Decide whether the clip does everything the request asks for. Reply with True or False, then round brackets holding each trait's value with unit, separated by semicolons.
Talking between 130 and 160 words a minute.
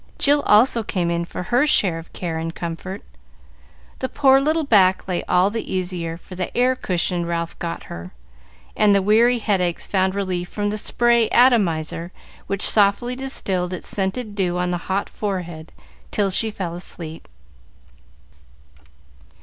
True (155 wpm)